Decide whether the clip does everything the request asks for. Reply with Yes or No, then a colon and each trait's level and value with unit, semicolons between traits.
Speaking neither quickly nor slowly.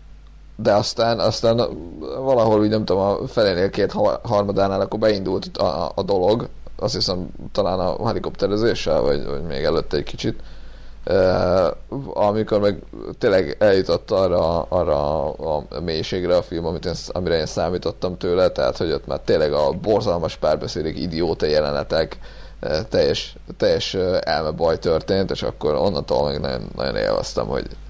Yes: average, 145 wpm